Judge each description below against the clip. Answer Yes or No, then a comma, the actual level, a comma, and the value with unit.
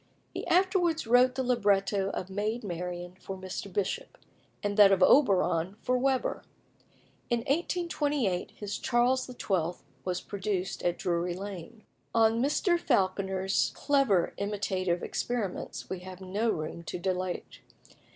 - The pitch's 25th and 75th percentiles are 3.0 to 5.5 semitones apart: Yes, average, 4.9 semitones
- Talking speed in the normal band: No, slow, 130 wpm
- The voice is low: No, high, 200 Hz